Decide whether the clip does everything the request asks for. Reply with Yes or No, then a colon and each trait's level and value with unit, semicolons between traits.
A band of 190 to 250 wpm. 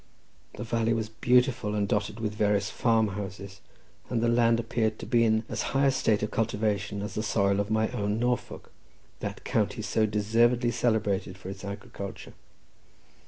No: average, 165 wpm